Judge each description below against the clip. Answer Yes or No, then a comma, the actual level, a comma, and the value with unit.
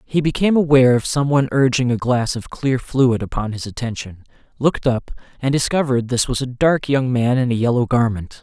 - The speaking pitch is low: Yes, low, 125 Hz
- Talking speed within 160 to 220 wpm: Yes, average, 200 wpm